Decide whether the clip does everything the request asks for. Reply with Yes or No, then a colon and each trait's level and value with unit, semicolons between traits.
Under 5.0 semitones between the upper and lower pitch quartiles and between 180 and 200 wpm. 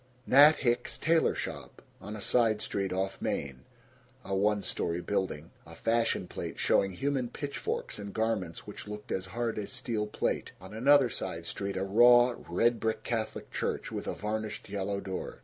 No: average, 3.7 semitones; average, 170 wpm